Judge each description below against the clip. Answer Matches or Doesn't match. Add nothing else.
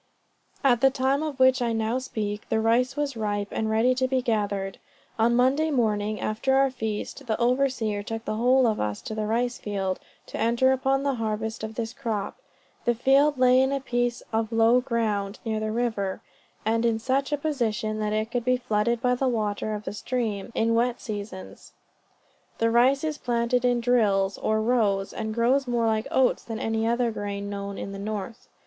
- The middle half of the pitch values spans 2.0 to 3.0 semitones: Matches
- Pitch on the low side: Doesn't match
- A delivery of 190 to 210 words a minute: Matches